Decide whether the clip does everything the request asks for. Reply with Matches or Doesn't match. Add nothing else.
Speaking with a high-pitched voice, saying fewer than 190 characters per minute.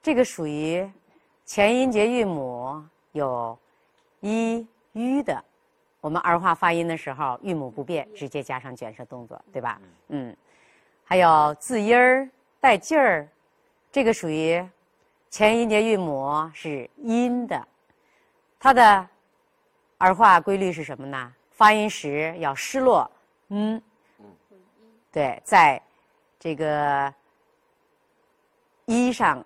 Matches